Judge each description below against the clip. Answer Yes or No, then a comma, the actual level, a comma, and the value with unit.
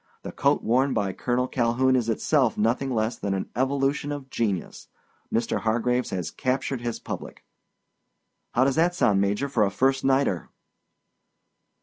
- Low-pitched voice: Yes, low, 125 Hz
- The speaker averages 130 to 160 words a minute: Yes, average, 150 wpm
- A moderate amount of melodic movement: Yes, average, 3.5 semitones